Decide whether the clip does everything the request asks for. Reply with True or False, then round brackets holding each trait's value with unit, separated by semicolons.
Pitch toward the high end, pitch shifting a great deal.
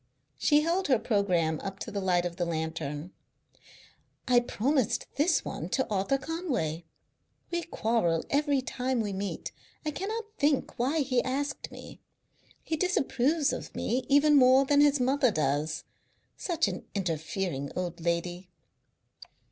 True (245 Hz; 8.5 semitones)